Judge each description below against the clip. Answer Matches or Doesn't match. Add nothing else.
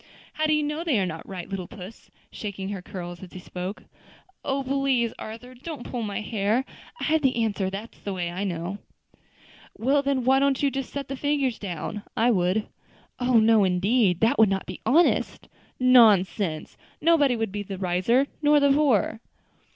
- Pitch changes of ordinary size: Doesn't match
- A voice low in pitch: Doesn't match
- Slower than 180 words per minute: Doesn't match